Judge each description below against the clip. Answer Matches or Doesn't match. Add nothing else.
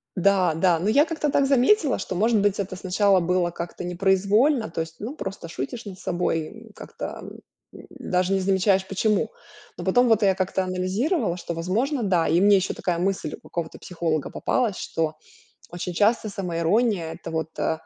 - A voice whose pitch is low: Doesn't match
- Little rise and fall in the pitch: Doesn't match